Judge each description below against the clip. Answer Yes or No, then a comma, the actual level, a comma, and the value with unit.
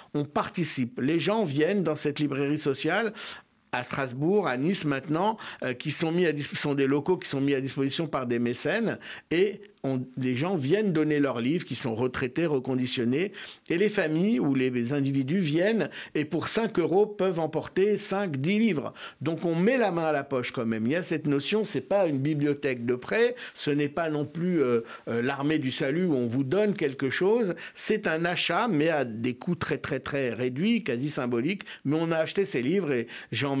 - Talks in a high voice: No, medium, 150 Hz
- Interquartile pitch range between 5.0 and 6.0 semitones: Yes, average, 5.3 semitones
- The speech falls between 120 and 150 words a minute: No, average, 210 wpm